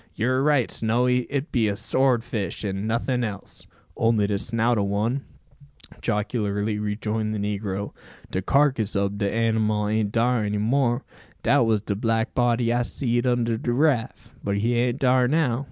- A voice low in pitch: Yes, low, 115 Hz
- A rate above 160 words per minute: Yes, average, 170 wpm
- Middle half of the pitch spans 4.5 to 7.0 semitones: No, average, 2.8 semitones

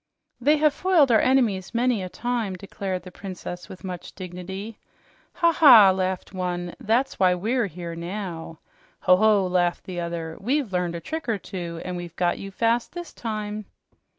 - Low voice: No, high, 190 Hz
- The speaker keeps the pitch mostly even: No, average, 4.5 semitones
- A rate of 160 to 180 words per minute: Yes, average, 175 wpm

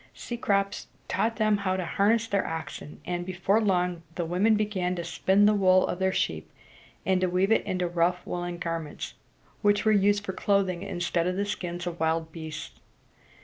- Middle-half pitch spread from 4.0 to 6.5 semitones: No, narrow, 2.6 semitones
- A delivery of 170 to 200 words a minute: Yes, average, 185 wpm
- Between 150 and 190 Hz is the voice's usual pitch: Yes, medium, 185 Hz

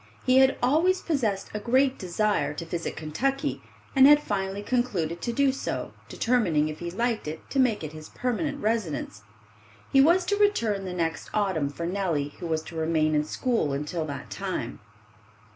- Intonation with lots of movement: Yes, wide, 8.3 semitones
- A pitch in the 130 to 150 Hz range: No, high, 205 Hz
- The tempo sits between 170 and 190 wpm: Yes, average, 175 wpm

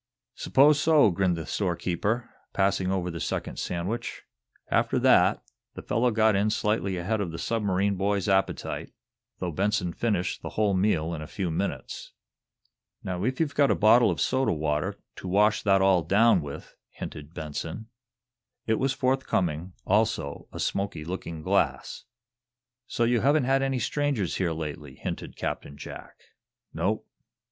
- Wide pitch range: No, average, 4.8 semitones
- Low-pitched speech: Yes, low, 100 Hz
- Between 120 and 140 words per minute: No, average, 155 wpm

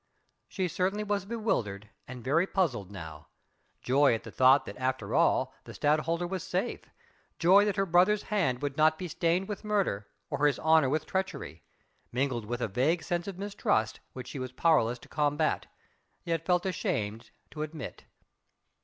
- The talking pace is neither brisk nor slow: Yes, average, 170 wpm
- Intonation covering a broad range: Yes, wide, 6.4 semitones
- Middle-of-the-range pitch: Yes, medium, 155 Hz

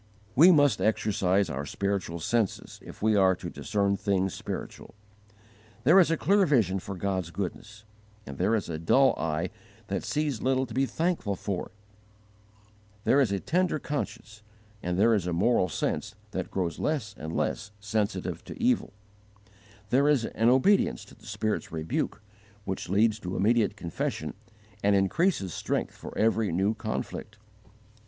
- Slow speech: No, average, 155 wpm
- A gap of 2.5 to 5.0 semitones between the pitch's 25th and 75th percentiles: No, wide, 5.5 semitones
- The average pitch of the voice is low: Yes, low, 105 Hz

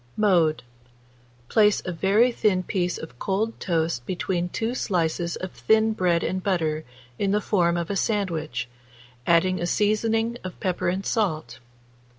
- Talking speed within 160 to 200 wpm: No, average, 150 wpm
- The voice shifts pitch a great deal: No, average, 3.6 semitones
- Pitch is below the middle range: No, medium, 185 Hz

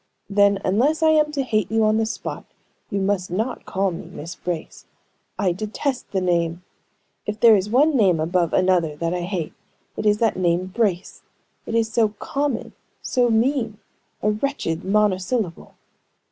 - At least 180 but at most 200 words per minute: No, average, 165 wpm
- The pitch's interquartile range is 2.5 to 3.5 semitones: No, average, 4.1 semitones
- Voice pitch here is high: Yes, high, 205 Hz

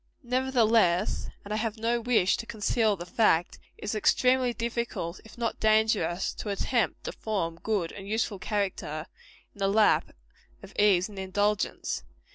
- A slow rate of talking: No, average, 155 wpm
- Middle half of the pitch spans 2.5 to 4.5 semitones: Yes, average, 3.1 semitones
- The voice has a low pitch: No, high, 210 Hz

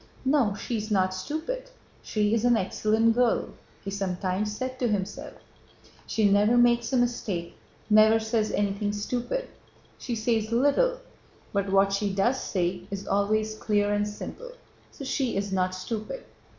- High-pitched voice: Yes, high, 215 Hz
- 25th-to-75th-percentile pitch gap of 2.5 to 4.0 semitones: Yes, average, 3.3 semitones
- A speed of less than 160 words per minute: Yes, average, 150 wpm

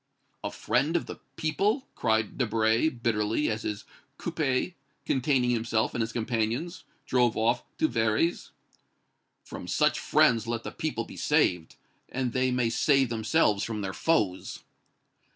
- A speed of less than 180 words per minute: Yes, slow, 135 wpm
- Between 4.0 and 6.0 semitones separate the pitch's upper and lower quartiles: No, average, 3.6 semitones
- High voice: No, low, 120 Hz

